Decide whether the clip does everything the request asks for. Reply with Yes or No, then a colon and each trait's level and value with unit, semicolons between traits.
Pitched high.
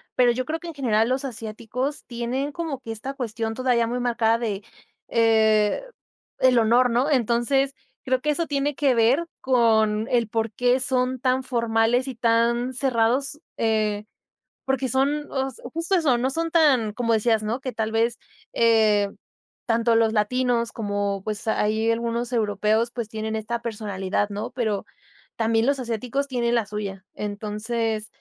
Yes: high, 235 Hz